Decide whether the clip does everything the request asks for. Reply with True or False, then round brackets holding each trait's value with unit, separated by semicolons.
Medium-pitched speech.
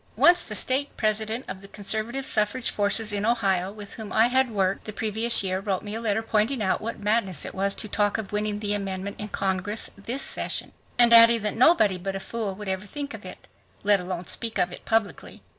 False (210 Hz)